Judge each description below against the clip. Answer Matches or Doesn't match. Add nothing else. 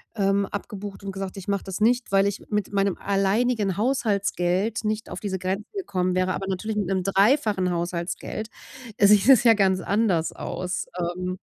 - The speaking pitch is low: Doesn't match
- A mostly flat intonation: Matches